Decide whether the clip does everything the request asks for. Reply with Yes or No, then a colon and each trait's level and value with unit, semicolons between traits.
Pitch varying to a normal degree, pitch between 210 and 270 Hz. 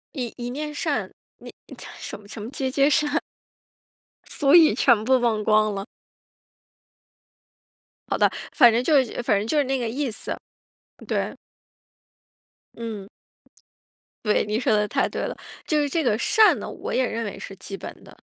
Yes: average, 4.7 semitones; high, 240 Hz